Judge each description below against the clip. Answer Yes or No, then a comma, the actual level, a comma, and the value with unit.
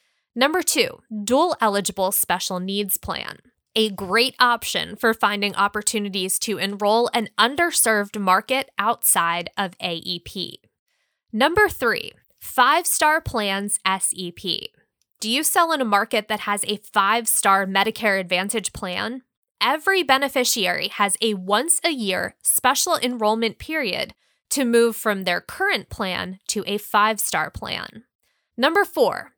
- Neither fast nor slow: No, slow, 130 wpm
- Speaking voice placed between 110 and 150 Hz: No, high, 220 Hz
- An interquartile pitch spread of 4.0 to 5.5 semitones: Yes, average, 4.5 semitones